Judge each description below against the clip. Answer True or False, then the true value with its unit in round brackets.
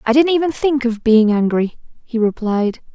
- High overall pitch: True (240 Hz)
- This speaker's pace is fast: False (185 wpm)